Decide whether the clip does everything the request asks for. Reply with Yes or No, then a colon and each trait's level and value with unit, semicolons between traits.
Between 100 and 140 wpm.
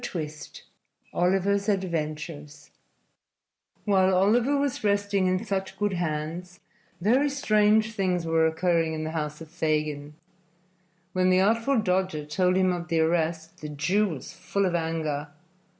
Yes: slow, 135 wpm